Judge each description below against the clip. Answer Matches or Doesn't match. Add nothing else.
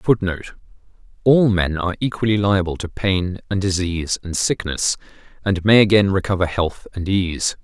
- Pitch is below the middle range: Matches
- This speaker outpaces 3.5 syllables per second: Matches